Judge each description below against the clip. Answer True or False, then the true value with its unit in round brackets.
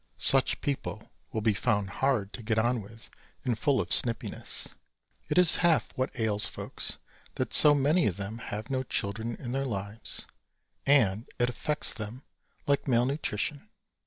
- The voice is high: False (120 Hz)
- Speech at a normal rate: True (160 wpm)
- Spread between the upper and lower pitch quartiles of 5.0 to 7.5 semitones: False (4.3 semitones)